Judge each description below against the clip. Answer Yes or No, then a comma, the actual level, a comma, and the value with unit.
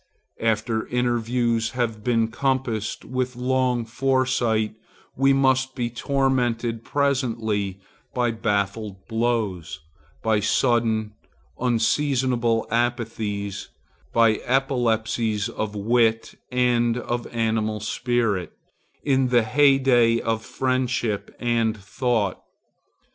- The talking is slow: Yes, slow, 90 wpm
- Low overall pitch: Yes, low, 115 Hz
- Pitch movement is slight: Yes, narrow, 2.2 semitones